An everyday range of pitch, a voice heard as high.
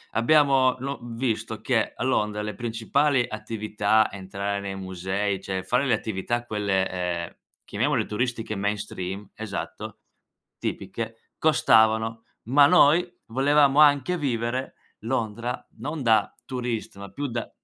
No: average, 4.3 semitones; low, 115 Hz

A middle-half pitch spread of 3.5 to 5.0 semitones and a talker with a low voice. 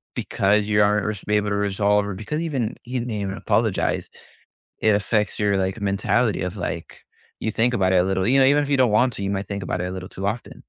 No: narrow, 2.6 semitones; low, 105 Hz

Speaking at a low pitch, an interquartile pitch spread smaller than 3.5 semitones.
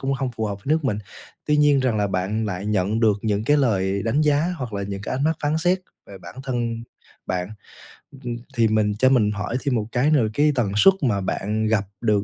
No: low, 115 Hz; average, 4.9 semitones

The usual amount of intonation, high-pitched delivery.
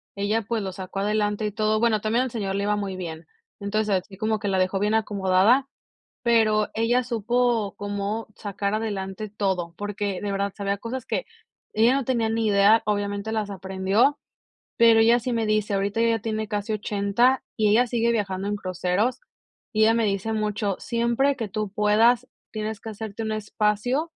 No: narrow, 2.1 semitones; high, 215 Hz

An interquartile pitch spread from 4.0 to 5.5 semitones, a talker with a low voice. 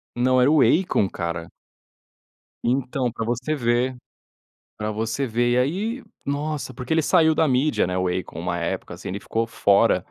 Yes: average, 5.1 semitones; low, 125 Hz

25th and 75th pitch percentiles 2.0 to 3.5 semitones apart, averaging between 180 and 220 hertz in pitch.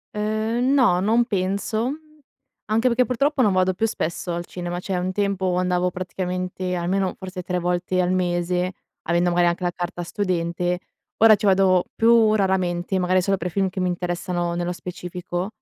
Yes: narrow, 2.3 semitones; medium, 185 Hz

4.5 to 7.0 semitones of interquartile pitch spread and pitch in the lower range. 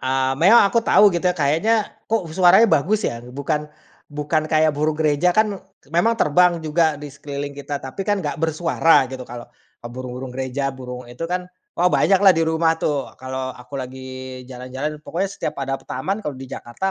No: average, 5.0 semitones; medium, 150 Hz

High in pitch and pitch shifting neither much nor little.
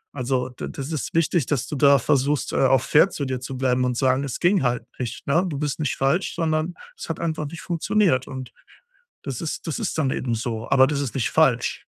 No: medium, 140 Hz; average, 3.5 semitones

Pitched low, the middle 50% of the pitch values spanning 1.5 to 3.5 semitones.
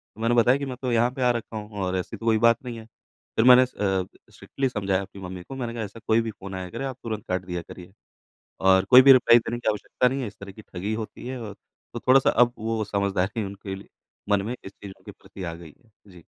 No: low, 110 Hz; average, 3.9 semitones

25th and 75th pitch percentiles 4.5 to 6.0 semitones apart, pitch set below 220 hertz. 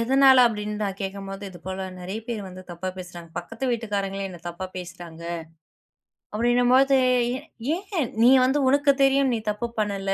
Yes: average, 4.9 semitones; high, 205 Hz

